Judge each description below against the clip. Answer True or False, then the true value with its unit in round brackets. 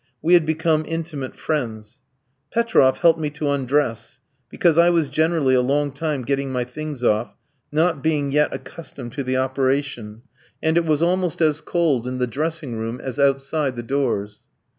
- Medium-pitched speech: True (145 Hz)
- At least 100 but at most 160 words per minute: False (170 wpm)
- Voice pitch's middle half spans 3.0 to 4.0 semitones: True (3.7 semitones)